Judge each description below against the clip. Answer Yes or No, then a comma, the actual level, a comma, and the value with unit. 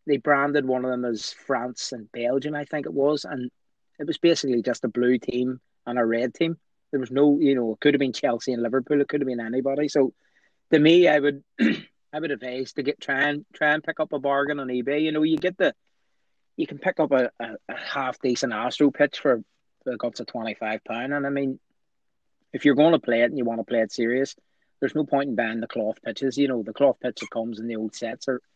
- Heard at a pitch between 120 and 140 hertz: Yes, low, 135 Hz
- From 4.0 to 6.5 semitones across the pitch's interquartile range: No, average, 3.0 semitones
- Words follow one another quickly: Yes, fast, 245 wpm